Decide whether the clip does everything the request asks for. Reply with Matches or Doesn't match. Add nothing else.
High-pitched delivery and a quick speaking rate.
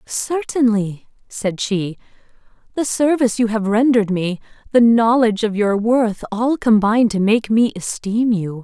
Doesn't match